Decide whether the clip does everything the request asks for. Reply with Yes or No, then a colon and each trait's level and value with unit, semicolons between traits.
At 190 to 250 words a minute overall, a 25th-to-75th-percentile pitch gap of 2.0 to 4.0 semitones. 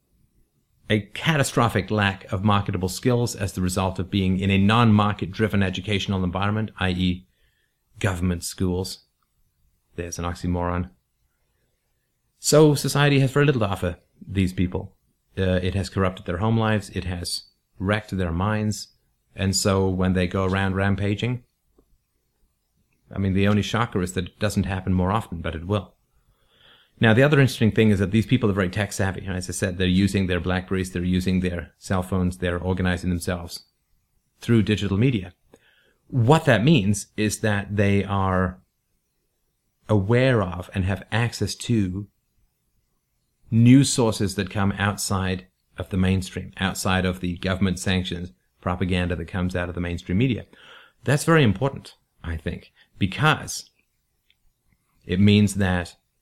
No: average, 150 wpm; average, 2.7 semitones